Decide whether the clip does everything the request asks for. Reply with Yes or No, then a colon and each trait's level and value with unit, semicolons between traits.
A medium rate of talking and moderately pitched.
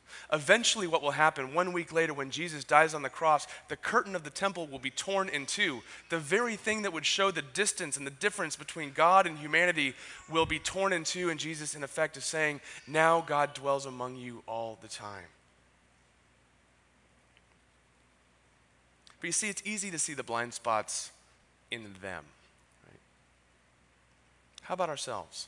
Yes: average, 170 wpm; medium, 145 Hz